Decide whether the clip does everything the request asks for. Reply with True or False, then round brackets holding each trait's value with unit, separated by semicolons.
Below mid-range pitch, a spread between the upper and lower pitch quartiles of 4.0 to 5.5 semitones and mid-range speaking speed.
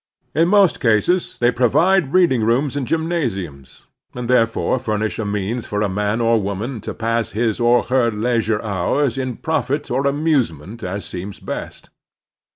True (115 Hz; 4.6 semitones; 170 wpm)